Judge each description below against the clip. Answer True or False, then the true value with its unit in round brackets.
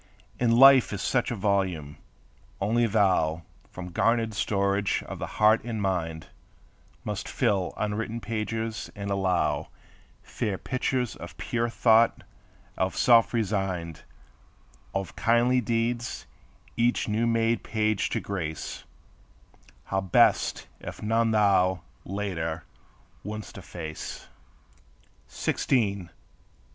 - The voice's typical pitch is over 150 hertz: False (105 Hz)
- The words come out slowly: True (110 wpm)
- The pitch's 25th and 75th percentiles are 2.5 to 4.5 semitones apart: True (3.4 semitones)